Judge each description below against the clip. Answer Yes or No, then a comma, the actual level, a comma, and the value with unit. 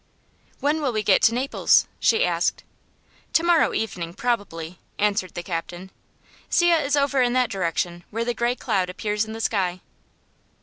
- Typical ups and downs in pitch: No, wide, 5.8 semitones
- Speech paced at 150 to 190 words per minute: Yes, average, 170 wpm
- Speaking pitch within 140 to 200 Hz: No, high, 220 Hz